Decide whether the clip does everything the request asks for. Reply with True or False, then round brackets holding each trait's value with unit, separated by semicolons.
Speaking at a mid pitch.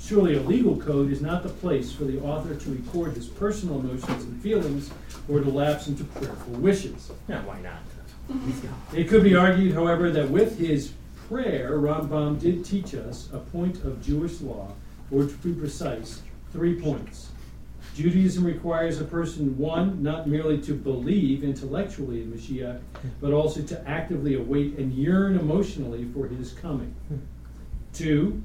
True (150 Hz)